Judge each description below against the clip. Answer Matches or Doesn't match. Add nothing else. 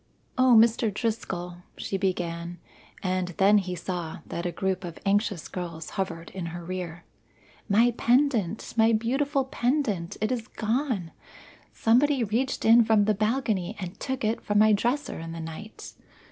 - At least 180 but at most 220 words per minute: Doesn't match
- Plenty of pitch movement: Doesn't match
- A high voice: Matches